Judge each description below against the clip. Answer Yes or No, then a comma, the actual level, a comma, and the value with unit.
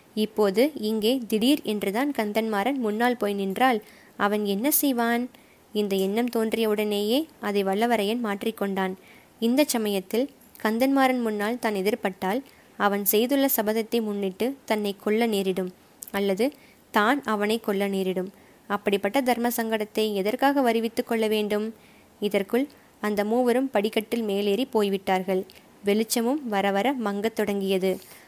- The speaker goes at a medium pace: Yes, average, 110 wpm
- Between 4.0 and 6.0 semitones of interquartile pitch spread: No, average, 2.8 semitones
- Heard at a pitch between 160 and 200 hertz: No, high, 215 Hz